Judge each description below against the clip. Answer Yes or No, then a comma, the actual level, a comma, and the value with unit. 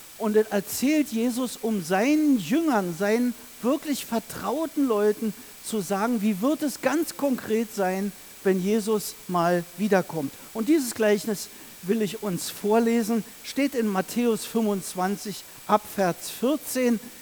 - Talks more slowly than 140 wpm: Yes, slow, 125 wpm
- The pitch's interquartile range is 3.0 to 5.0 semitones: Yes, average, 3.3 semitones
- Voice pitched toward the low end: No, high, 220 Hz